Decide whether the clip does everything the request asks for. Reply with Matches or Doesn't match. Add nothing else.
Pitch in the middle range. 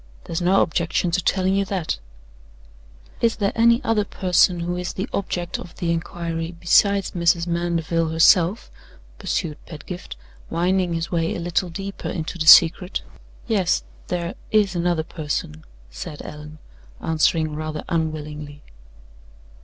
Matches